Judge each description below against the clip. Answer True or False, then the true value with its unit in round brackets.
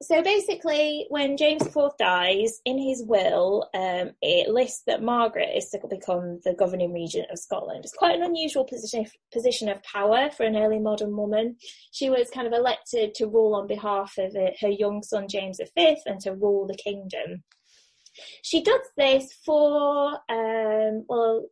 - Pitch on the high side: True (225 Hz)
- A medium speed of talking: True (170 wpm)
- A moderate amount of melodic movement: False (5.8 semitones)